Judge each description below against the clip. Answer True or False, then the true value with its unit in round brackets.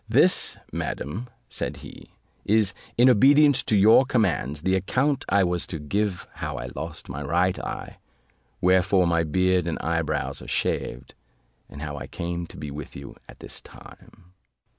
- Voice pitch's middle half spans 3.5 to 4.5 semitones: False (5.1 semitones)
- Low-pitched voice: True (90 Hz)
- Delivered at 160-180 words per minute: True (165 wpm)